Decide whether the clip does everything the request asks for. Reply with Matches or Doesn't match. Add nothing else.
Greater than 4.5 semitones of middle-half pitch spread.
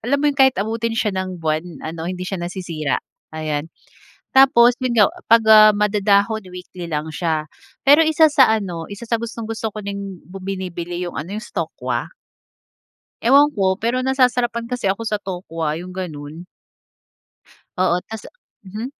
Matches